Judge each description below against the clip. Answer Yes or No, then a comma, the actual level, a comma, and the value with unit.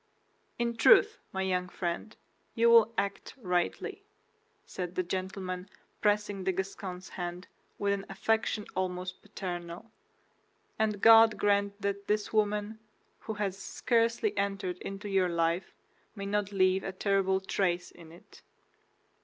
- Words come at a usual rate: No, slow, 130 wpm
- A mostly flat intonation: Yes, narrow, 2.2 semitones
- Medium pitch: No, high, 195 Hz